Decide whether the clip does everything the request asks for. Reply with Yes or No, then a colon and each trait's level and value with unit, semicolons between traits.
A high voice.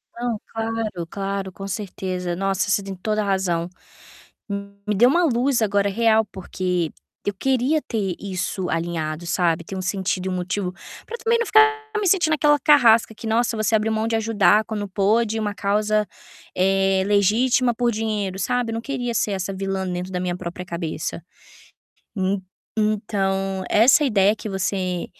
Yes: high, 200 Hz